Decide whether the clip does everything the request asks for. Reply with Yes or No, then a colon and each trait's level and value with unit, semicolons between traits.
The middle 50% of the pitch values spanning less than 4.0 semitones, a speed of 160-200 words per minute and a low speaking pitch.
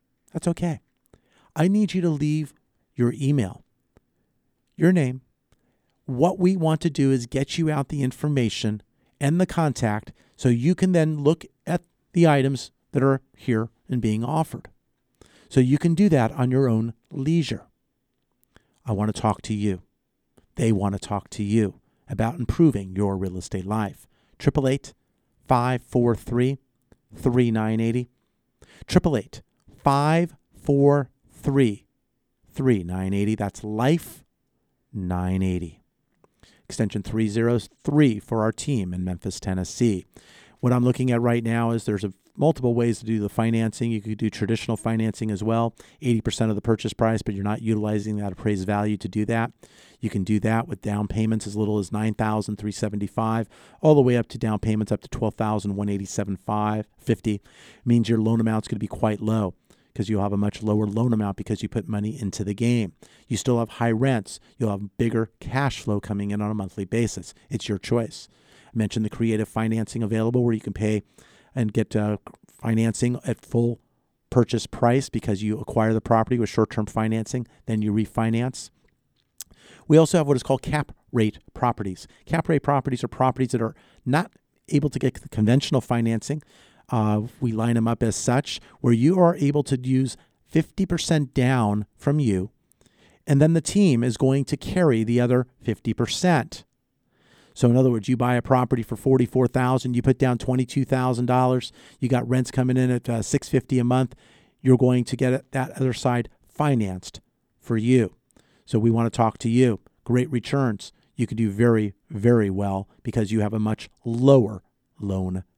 Yes: average, 3.5 semitones; average, 175 wpm; low, 115 Hz